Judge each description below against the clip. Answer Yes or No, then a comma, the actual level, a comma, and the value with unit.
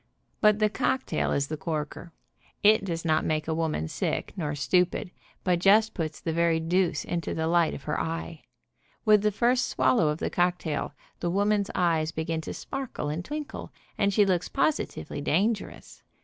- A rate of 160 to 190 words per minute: Yes, average, 175 wpm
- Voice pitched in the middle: Yes, medium, 170 Hz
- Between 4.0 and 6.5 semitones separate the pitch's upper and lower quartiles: Yes, average, 4.3 semitones